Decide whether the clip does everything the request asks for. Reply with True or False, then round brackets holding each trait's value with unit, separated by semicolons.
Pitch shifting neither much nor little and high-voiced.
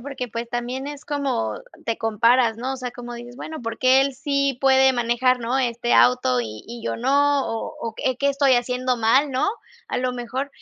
False (2.2 semitones; 250 Hz)